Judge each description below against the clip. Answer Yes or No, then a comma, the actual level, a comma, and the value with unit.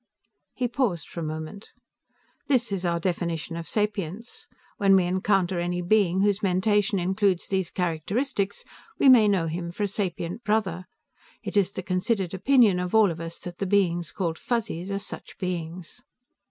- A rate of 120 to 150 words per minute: No, average, 165 wpm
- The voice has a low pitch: No, high, 190 Hz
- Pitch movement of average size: Yes, average, 3.1 semitones